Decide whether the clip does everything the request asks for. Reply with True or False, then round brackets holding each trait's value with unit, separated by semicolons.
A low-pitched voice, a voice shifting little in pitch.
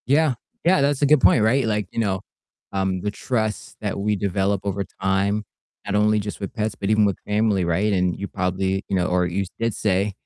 True (100 Hz; 2.0 semitones)